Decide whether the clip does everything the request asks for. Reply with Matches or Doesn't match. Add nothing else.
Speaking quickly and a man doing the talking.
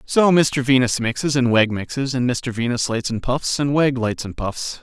Matches